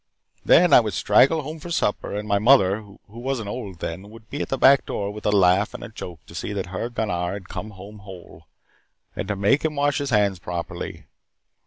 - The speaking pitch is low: Yes, low, 105 Hz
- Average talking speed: No, fast, 220 wpm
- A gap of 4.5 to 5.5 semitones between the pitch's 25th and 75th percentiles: Yes, average, 4.9 semitones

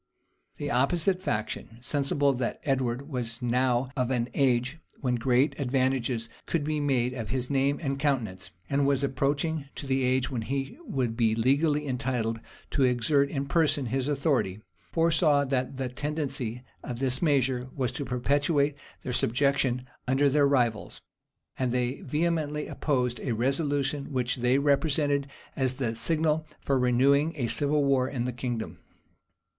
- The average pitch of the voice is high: No, low, 135 Hz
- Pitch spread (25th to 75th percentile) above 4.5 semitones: No, narrow, 2.5 semitones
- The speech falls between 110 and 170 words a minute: Yes, average, 155 wpm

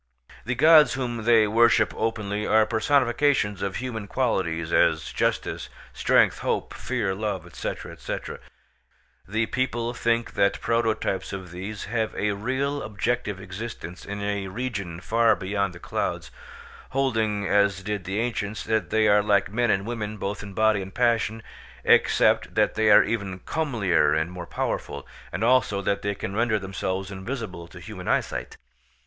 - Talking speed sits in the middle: Yes, average, 155 wpm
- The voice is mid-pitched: No, low, 105 Hz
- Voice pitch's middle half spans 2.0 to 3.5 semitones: Yes, average, 3.2 semitones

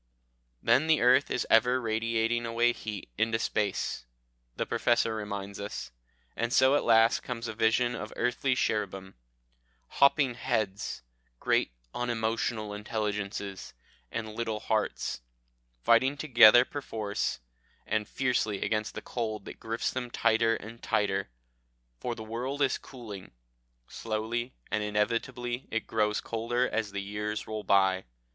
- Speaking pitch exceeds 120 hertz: No, low, 115 Hz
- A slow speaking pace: Yes, slow, 130 wpm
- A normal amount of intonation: No, narrow, 2.3 semitones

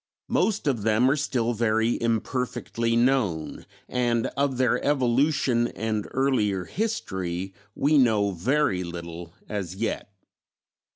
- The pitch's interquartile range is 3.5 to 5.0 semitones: Yes, average, 4.7 semitones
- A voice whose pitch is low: Yes, low, 115 Hz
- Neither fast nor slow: No, slow, 115 wpm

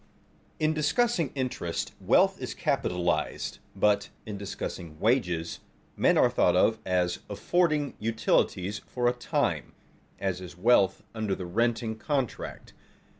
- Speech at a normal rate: No, slow, 125 wpm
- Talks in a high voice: No, low, 110 Hz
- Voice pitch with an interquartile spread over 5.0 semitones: Yes, wide, 5.6 semitones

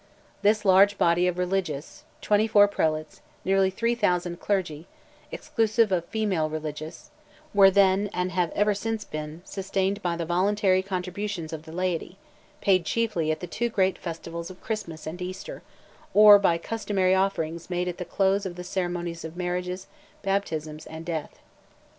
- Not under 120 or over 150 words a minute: Yes, average, 145 wpm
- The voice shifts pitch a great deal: No, average, 3.0 semitones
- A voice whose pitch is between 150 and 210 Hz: Yes, medium, 185 Hz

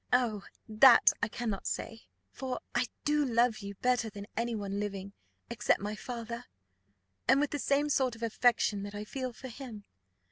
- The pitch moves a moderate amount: Yes, average, 3.3 semitones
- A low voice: No, high, 235 Hz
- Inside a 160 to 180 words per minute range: Yes, average, 175 wpm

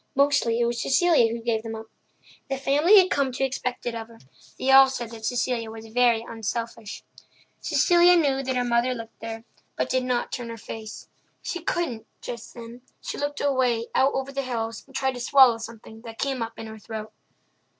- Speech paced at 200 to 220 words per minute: Yes, fast, 205 wpm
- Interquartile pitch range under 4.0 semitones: Yes, average, 2.9 semitones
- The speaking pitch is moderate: No, high, 240 Hz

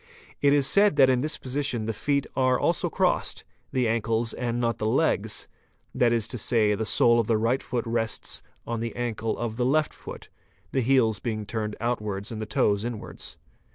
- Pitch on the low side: Yes, low, 115 Hz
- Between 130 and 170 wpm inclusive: No, average, 195 wpm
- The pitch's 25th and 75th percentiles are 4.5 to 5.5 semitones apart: No, narrow, 2.6 semitones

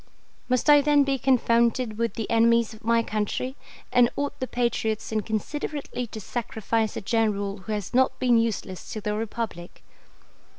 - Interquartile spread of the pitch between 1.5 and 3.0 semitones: Yes, narrow, 2.5 semitones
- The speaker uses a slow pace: No, average, 160 wpm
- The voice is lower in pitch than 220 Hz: No, high, 230 Hz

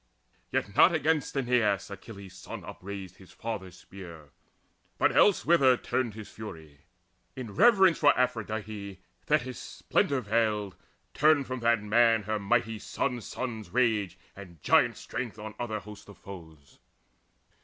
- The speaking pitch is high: No, low, 110 Hz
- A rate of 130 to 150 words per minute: Yes, slow, 135 wpm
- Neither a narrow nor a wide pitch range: Yes, average, 4.1 semitones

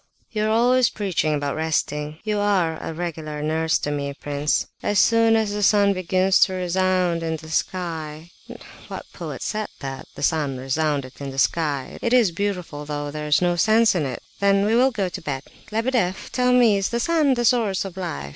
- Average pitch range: No, wide, 5.7 semitones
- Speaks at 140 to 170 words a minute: No, average, 190 wpm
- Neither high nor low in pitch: Yes, medium, 180 Hz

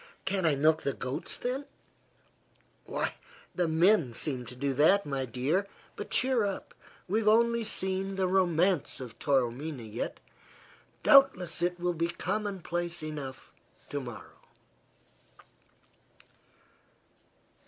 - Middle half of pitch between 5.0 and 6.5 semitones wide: Yes, wide, 5.6 semitones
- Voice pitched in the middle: Yes, medium, 175 Hz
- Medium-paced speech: No, slow, 110 wpm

